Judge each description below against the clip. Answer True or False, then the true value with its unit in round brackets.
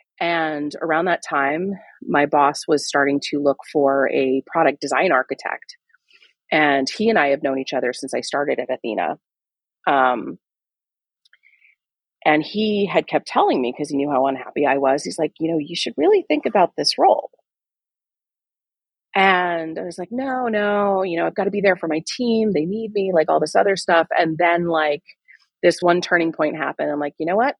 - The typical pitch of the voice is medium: True (165 Hz)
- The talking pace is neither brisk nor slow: True (195 wpm)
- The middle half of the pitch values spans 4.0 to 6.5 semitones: True (5.4 semitones)